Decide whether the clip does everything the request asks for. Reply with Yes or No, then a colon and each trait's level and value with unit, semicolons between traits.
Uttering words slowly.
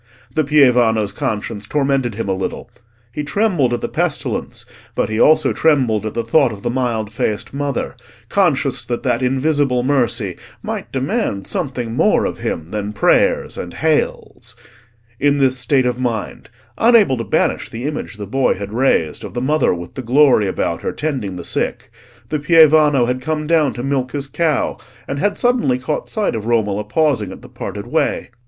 No: average, 175 wpm